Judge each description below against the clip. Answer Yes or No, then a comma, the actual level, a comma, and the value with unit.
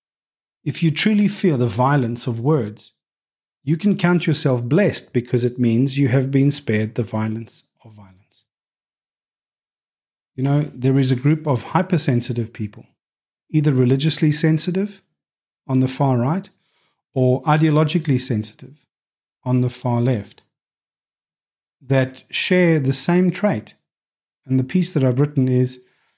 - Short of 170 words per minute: Yes, slow, 135 wpm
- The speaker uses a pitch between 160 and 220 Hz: No, low, 135 Hz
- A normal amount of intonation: Yes, average, 4.2 semitones